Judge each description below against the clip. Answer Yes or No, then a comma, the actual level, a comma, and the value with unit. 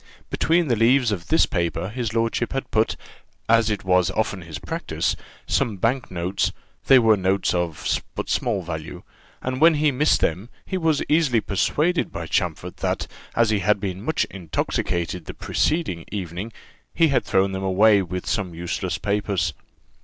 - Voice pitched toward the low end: Yes, low, 105 Hz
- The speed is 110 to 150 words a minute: No, average, 170 wpm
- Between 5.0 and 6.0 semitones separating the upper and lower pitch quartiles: Yes, wide, 5.4 semitones